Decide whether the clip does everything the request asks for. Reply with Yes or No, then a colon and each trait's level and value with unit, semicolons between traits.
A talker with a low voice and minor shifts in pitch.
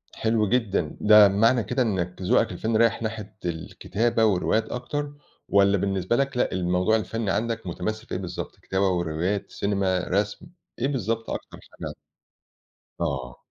No: low, 105 Hz; average, 3.6 semitones